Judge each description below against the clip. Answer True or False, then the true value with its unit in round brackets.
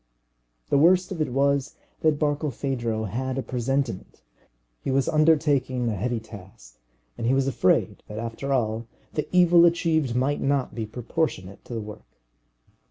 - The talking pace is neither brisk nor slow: True (155 wpm)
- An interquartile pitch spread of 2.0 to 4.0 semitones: False (4.5 semitones)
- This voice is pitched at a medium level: False (130 Hz)